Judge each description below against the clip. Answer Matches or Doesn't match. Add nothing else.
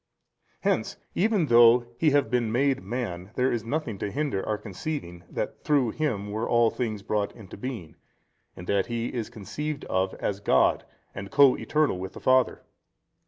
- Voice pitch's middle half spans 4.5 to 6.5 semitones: Matches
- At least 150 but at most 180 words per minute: Matches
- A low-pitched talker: Matches